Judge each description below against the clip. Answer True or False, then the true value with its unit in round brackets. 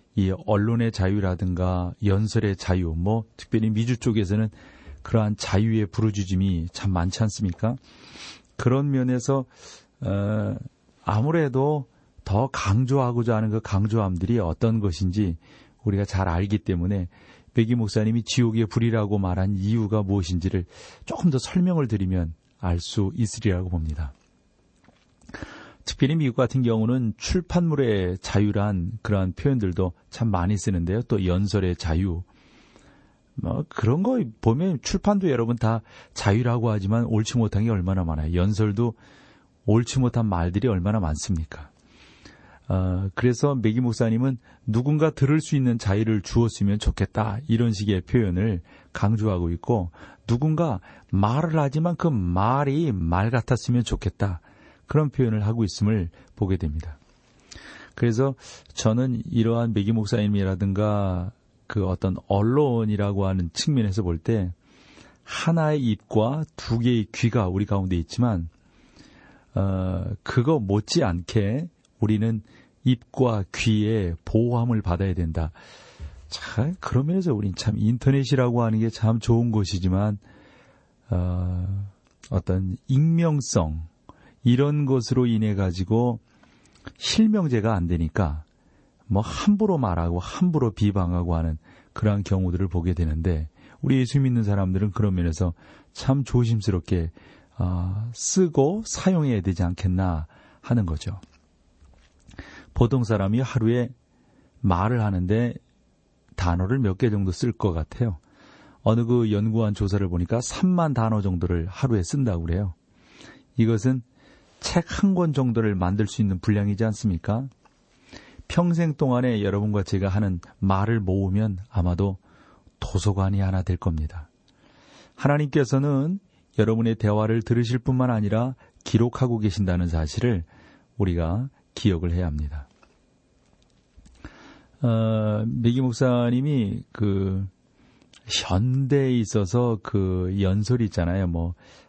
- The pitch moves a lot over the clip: False (4.5 semitones)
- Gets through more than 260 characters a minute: True (270 characters per minute)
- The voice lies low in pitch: True (105 Hz)